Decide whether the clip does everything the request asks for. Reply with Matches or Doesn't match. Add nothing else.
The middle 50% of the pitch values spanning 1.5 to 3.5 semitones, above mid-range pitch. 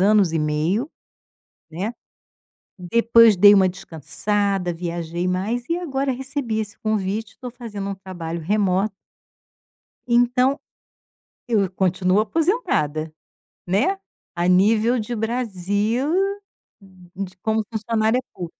Doesn't match